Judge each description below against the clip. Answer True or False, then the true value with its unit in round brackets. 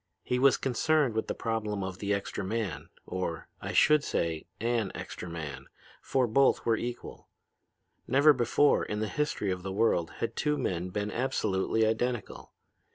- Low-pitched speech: True (110 Hz)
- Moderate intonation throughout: True (4.8 semitones)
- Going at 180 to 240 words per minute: False (160 wpm)